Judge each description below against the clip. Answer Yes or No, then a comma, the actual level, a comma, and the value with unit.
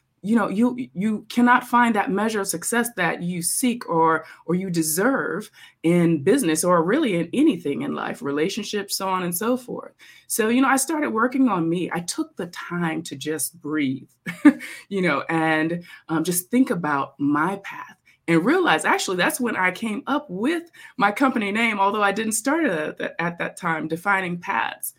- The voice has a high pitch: Yes, high, 195 Hz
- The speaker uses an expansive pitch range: Yes, wide, 6.6 semitones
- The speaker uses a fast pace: No, average, 180 wpm